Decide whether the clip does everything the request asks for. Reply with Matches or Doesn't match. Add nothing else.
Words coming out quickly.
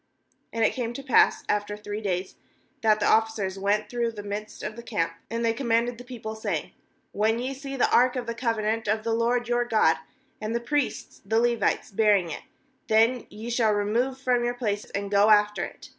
Matches